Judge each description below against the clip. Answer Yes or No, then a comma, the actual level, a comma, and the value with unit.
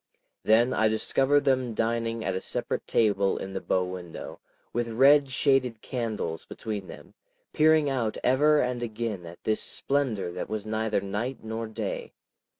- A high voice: No, low, 115 Hz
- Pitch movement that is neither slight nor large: Yes, average, 3.8 semitones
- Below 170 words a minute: Yes, average, 155 wpm